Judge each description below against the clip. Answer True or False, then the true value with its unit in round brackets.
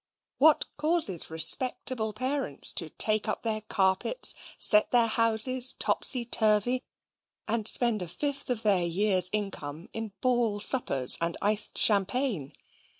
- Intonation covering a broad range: False (4.4 semitones)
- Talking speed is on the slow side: True (130 wpm)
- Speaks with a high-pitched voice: True (215 Hz)